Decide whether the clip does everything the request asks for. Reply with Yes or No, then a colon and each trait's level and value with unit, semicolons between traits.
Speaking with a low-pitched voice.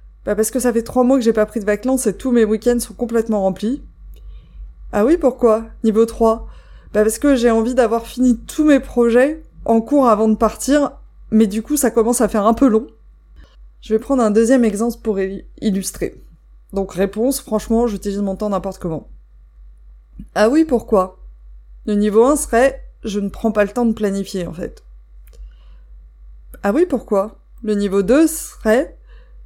No: high, 220 Hz